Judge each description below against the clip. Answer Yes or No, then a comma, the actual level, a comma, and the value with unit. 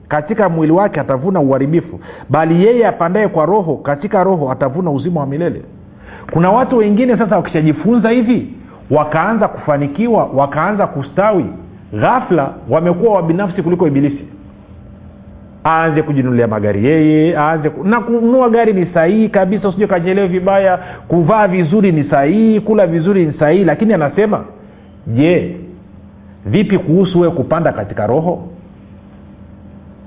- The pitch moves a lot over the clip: Yes, wide, 6.2 semitones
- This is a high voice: No, medium, 165 Hz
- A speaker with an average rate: Yes, average, 120 wpm